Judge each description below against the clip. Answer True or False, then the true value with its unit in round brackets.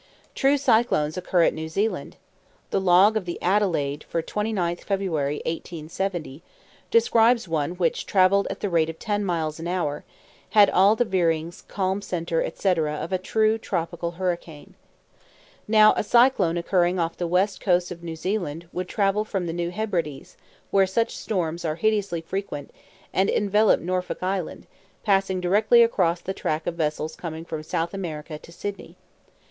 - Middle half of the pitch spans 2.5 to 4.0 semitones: True (3.3 semitones)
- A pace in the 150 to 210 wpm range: True (165 wpm)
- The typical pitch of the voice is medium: True (180 Hz)